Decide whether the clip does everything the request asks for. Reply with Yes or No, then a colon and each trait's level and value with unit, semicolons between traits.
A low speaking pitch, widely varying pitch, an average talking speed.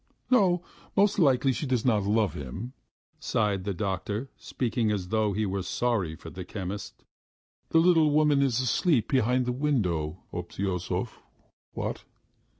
Yes: low, 110 Hz; wide, 5.9 semitones; average, 145 wpm